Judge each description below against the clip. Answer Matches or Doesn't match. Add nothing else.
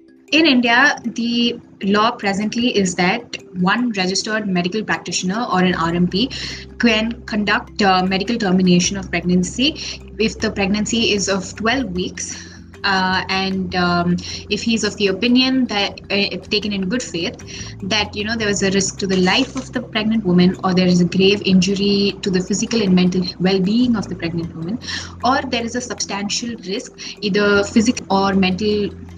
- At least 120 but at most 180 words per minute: Matches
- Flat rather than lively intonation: Doesn't match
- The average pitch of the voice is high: Matches